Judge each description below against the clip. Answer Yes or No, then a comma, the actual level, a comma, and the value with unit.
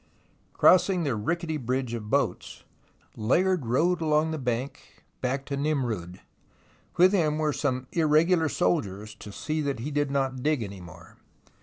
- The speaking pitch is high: No, medium, 140 Hz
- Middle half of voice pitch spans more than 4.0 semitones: Yes, average, 5.1 semitones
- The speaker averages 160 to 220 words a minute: No, average, 150 wpm